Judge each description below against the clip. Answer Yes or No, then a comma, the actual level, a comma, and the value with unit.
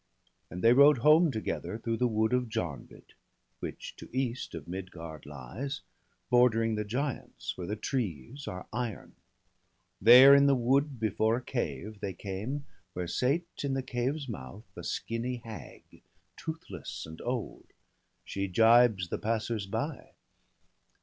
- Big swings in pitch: No, average, 4.7 semitones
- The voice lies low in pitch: Yes, low, 115 Hz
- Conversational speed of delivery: Yes, average, 145 wpm